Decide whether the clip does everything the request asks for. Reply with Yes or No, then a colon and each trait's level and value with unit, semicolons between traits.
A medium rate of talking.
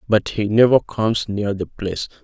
Yes: average, 190 wpm